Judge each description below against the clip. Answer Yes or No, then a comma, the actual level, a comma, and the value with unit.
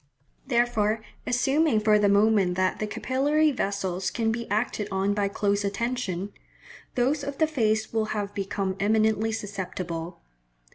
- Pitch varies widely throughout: No, average, 3.2 semitones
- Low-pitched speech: No, high, 215 Hz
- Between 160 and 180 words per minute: No, average, 140 wpm